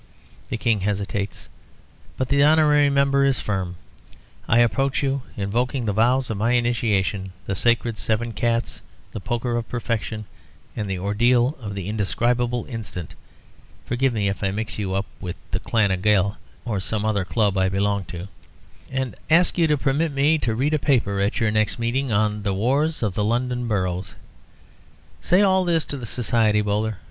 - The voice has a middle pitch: No, low, 115 Hz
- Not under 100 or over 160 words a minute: No, average, 175 wpm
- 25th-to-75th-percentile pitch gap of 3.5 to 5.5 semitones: Yes, average, 4.2 semitones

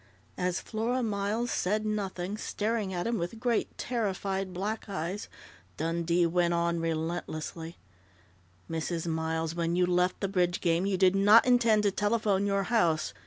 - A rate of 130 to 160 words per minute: Yes, average, 150 wpm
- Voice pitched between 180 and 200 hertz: Yes, high, 190 Hz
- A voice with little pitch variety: No, average, 3.7 semitones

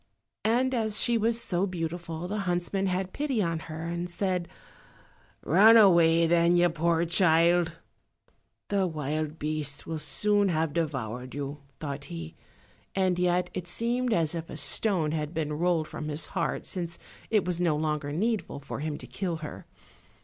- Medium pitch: Yes, medium, 170 Hz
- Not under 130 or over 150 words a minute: No, average, 165 wpm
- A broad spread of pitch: No, average, 3.4 semitones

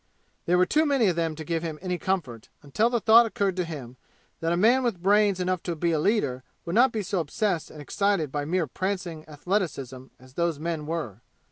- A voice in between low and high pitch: Yes, medium, 170 Hz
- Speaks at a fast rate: Yes, fast, 220 wpm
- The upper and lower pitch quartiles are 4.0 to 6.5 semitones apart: Yes, average, 4.7 semitones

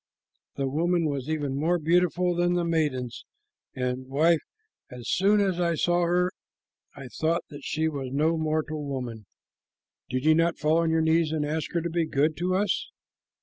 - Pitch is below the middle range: No, medium, 160 Hz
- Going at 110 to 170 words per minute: No, average, 180 wpm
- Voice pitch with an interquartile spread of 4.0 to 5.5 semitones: No, average, 3.3 semitones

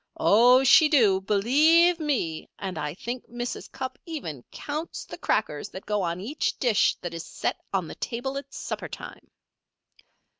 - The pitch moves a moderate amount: No, wide, 6.6 semitones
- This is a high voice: Yes, high, 240 Hz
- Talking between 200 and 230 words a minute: No, average, 160 wpm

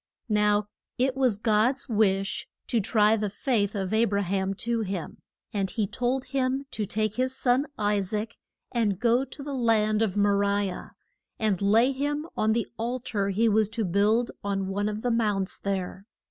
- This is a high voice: Yes, high, 215 Hz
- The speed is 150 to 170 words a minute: No, average, 190 wpm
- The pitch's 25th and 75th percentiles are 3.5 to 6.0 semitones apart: No, average, 3.0 semitones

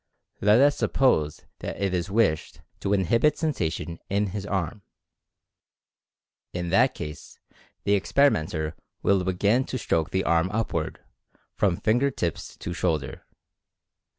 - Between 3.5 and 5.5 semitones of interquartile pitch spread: Yes, average, 5.1 semitones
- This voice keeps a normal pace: No, slow, 125 wpm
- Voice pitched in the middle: No, very low, 95 Hz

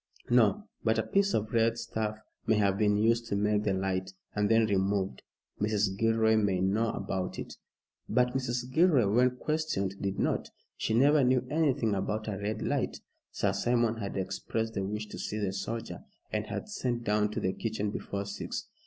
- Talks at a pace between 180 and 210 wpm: Yes, average, 185 wpm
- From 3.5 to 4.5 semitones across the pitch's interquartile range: No, average, 2.8 semitones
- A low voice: Yes, low, 110 Hz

